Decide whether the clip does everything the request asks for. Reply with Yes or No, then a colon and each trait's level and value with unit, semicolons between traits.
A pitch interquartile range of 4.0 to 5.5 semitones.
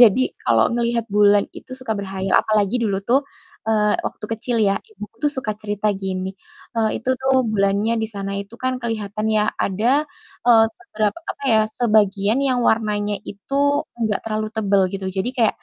No: average, 2.8 semitones